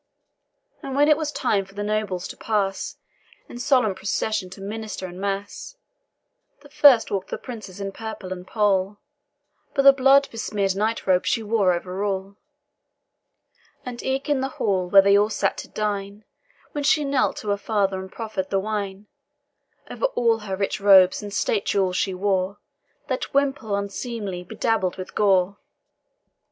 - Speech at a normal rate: Yes, average, 165 wpm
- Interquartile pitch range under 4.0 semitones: Yes, average, 2.9 semitones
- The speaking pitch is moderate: No, high, 205 Hz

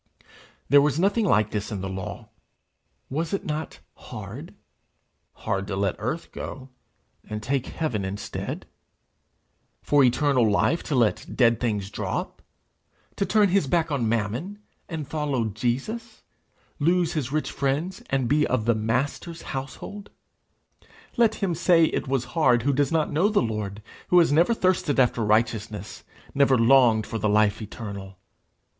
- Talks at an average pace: Yes, average, 150 wpm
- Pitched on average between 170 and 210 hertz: No, low, 135 Hz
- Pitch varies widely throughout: Yes, wide, 6.7 semitones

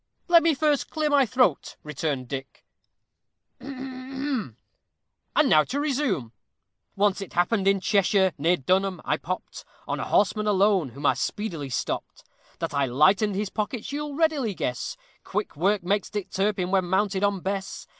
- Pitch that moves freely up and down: Yes, wide, 6.3 semitones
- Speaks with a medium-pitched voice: No, high, 200 Hz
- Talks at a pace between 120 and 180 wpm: Yes, average, 155 wpm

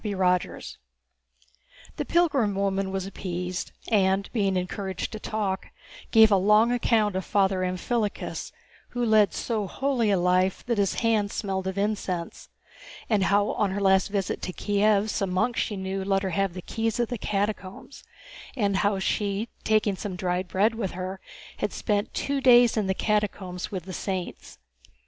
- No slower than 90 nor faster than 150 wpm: No, average, 170 wpm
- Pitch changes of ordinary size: No, narrow, 2.3 semitones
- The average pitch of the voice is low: No, high, 200 Hz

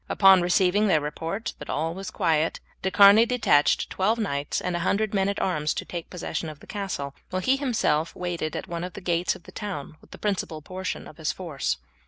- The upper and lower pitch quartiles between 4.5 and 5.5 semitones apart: No, average, 3.9 semitones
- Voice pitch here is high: No, medium, 180 Hz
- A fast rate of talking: Yes, fast, 220 wpm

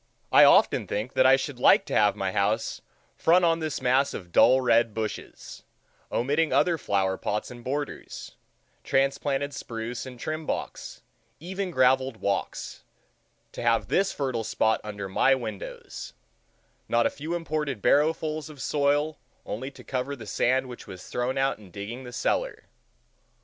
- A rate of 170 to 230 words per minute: No, average, 155 wpm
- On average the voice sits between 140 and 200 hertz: No, low, 130 Hz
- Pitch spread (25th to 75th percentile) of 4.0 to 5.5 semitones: Yes, average, 4.6 semitones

